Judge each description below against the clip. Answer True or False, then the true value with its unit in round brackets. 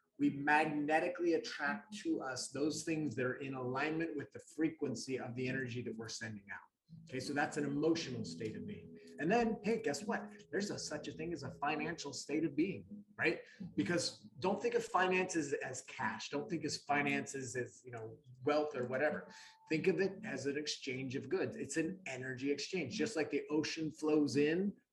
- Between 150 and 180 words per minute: False (195 wpm)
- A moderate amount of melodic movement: True (4.0 semitones)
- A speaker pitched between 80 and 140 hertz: False (150 Hz)